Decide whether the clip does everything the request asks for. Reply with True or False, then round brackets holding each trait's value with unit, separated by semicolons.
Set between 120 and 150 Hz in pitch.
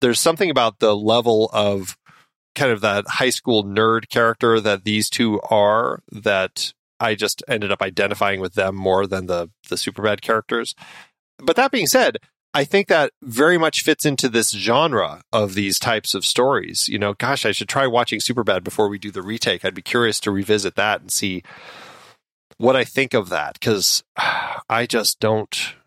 False (110 Hz)